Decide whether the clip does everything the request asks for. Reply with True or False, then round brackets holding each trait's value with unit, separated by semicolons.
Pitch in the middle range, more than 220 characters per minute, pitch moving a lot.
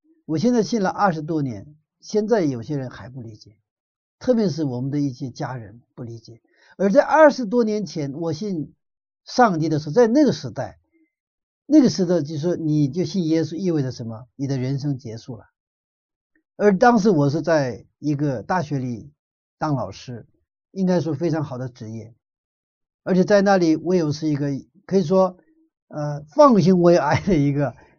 True (160 Hz; 255 characters per minute; 6.2 semitones)